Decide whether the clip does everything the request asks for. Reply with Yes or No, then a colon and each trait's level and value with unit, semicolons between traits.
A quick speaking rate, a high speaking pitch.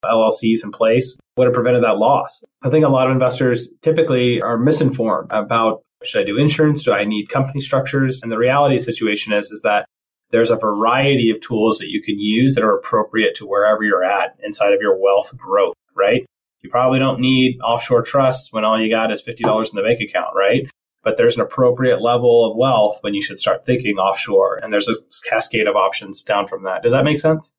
No: fast, 220 wpm; low, 125 Hz